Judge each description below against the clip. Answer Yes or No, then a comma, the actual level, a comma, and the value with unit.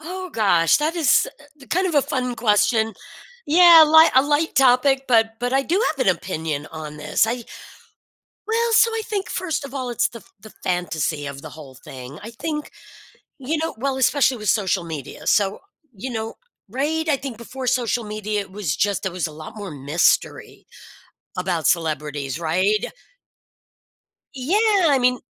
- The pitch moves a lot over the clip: Yes, wide, 8.1 semitones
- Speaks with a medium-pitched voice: No, high, 230 Hz